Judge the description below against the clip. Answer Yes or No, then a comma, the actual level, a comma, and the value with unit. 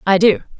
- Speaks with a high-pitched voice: Yes, high, 200 Hz